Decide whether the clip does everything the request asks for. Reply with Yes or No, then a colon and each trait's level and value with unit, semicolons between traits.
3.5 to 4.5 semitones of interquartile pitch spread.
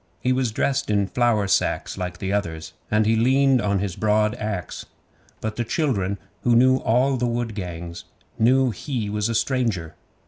Yes: average, 3.9 semitones